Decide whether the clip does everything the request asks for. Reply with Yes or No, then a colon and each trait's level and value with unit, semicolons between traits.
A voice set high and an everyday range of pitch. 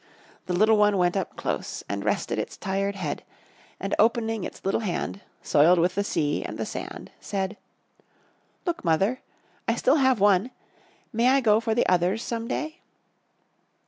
Yes: high, 205 Hz; average, 3.8 semitones